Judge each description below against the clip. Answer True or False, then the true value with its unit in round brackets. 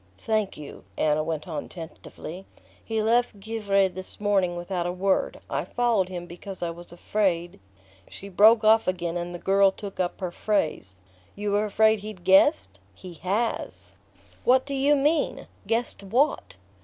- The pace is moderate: True (160 wpm)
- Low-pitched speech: False (195 Hz)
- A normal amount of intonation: True (3.7 semitones)